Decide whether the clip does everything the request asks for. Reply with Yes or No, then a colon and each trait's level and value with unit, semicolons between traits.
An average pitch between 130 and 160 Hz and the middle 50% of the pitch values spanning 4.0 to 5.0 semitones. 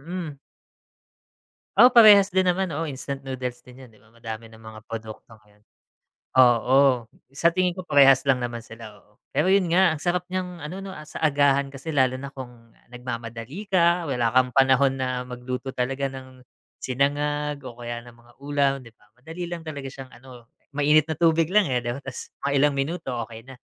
Yes: low, 135 Hz; average, 4.5 semitones